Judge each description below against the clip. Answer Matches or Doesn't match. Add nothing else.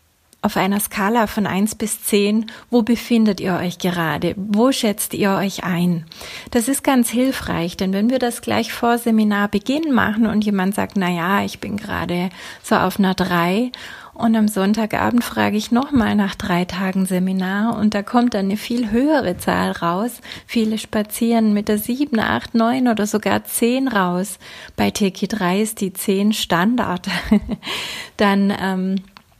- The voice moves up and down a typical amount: Matches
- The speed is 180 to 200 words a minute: Doesn't match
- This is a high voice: Matches